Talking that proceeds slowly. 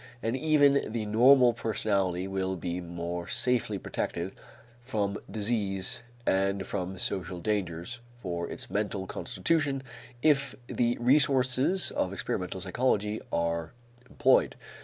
Yes: slow, 115 wpm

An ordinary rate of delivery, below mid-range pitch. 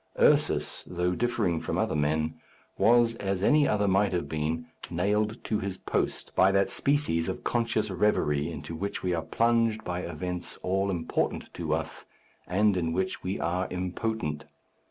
Yes: average, 160 wpm; very low, 95 Hz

